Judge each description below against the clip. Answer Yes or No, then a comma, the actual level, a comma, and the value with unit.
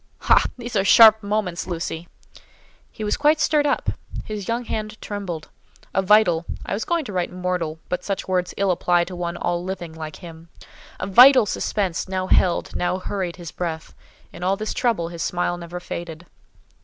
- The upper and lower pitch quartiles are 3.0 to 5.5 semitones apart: Yes, average, 3.6 semitones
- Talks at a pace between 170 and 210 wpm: Yes, average, 180 wpm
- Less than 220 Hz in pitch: Yes, medium, 185 Hz